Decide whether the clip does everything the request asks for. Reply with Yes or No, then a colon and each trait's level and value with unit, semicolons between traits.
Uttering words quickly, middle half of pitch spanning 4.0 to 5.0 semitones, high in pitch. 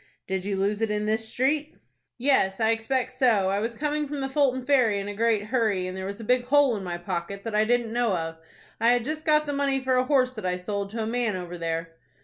Yes: fast, 260 wpm; average, 4.6 semitones; high, 225 Hz